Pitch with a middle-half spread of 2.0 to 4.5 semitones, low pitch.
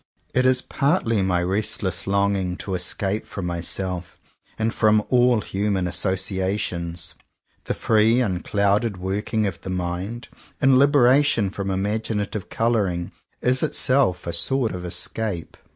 Yes: average, 3.9 semitones; low, 100 Hz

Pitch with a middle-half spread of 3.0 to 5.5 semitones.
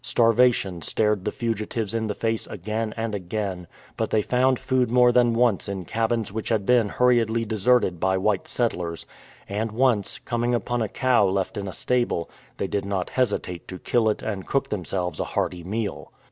Yes: average, 3.5 semitones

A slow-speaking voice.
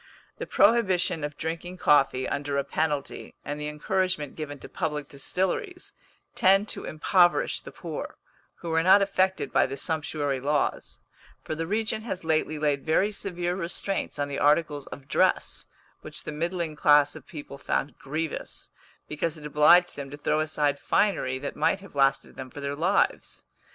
No: average, 165 wpm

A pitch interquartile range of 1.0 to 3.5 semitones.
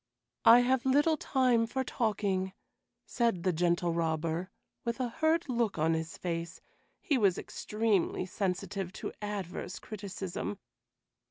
No: average, 5.3 semitones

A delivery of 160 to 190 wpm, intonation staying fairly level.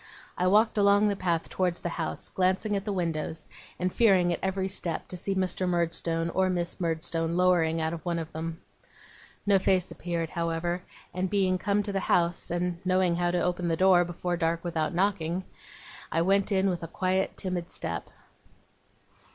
Yes: average, 185 wpm; narrow, 2.1 semitones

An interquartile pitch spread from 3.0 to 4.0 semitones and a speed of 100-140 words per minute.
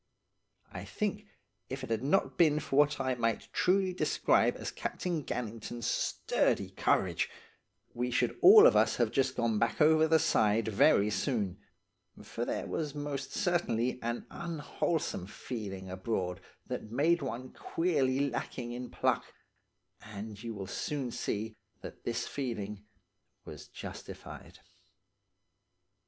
No: wide, 5.5 semitones; slow, 135 wpm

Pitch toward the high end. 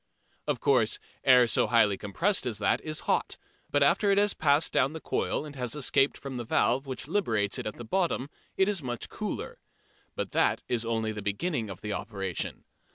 No: low, 125 Hz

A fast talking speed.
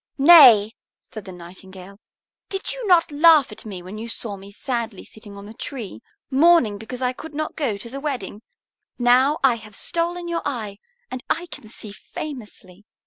No: average, 180 wpm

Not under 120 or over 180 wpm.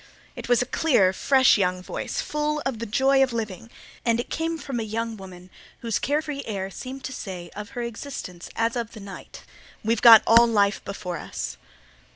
No: average, 190 wpm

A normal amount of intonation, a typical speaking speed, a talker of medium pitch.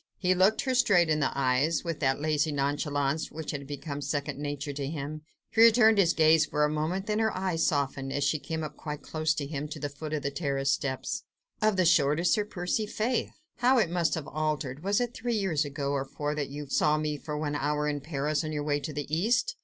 No: average, 3.5 semitones; fast, 235 wpm; medium, 150 Hz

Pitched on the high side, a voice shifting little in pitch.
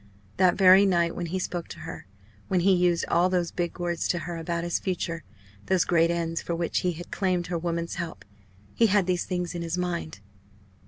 No: medium, 175 Hz; narrow, 1.2 semitones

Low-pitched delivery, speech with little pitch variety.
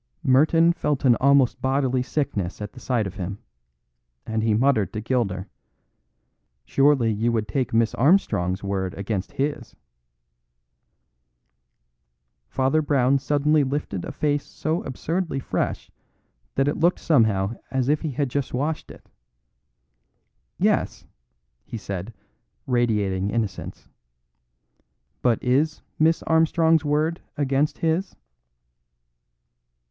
No: low, 130 Hz; wide, 5.4 semitones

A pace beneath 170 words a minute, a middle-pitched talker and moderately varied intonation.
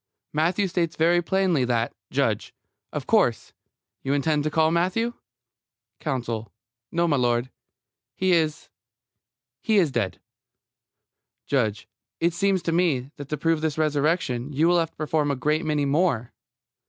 Yes: average, 140 wpm; medium, 155 Hz; average, 4.0 semitones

